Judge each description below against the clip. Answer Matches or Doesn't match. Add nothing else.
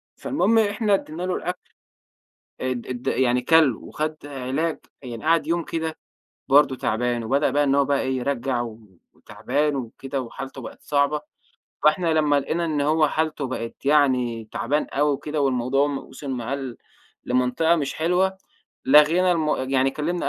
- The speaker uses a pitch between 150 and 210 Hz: Doesn't match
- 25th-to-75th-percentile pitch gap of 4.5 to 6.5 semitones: Doesn't match